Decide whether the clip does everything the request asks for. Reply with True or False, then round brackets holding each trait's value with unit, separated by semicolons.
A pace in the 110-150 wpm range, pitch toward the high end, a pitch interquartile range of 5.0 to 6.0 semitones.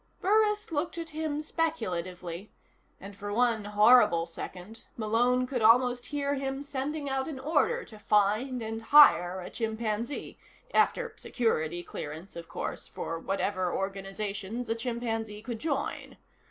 True (135 wpm; 225 Hz; 5.6 semitones)